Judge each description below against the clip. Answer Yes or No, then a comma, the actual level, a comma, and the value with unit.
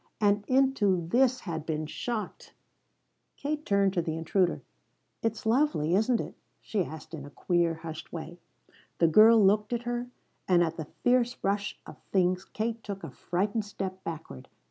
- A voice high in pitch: Yes, high, 195 Hz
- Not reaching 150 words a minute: No, average, 165 wpm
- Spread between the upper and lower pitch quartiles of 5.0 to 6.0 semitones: Yes, average, 5.3 semitones